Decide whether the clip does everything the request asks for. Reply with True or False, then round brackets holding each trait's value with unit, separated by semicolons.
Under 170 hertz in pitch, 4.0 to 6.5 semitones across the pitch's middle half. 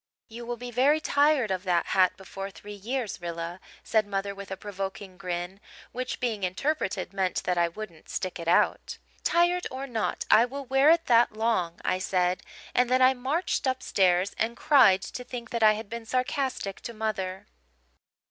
False (215 Hz; 5.2 semitones)